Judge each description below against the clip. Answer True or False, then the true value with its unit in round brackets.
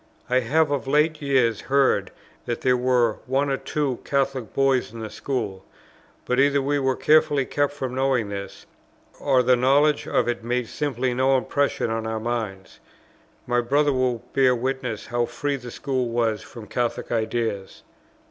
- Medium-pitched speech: False (130 Hz)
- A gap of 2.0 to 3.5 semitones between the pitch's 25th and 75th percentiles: True (2.8 semitones)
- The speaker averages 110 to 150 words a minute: False (165 wpm)